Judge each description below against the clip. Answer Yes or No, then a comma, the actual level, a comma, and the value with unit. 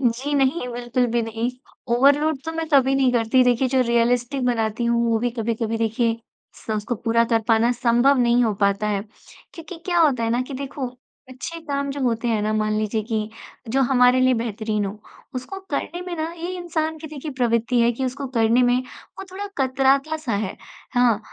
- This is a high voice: Yes, high, 245 Hz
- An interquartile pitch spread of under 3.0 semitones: No, average, 3.3 semitones